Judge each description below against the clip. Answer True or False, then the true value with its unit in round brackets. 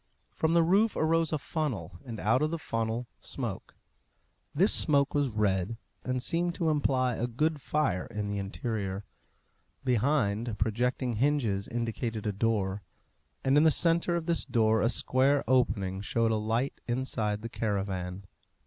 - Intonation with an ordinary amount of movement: False (5.7 semitones)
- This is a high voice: False (120 Hz)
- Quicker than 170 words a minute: False (155 wpm)